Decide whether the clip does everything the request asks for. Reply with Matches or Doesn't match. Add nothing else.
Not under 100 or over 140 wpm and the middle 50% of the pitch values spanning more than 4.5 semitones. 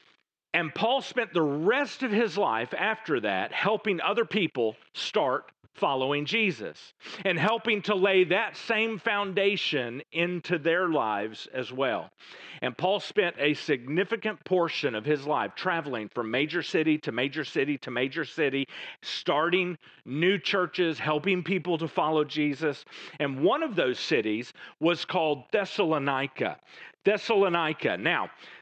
Matches